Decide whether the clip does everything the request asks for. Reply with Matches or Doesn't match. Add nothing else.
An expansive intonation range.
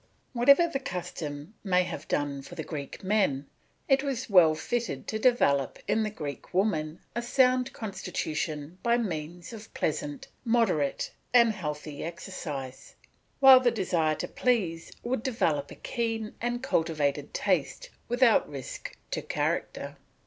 Matches